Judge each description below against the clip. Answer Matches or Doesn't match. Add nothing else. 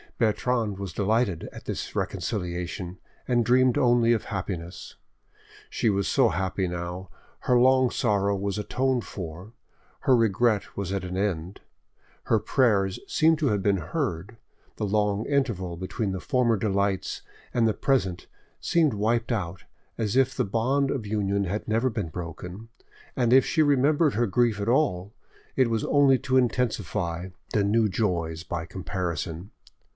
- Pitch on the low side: Matches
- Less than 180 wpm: Matches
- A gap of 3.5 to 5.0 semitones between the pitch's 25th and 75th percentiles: Matches